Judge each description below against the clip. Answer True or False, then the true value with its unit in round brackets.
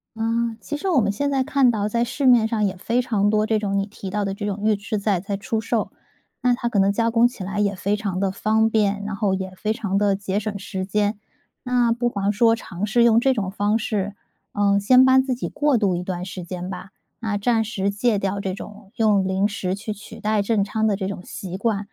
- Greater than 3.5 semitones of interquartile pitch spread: False (2.5 semitones)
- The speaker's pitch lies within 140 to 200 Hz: False (210 Hz)